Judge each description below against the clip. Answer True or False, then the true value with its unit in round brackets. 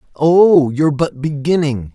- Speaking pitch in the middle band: True (150 Hz)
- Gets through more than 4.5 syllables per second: False (4.3 syllables/s)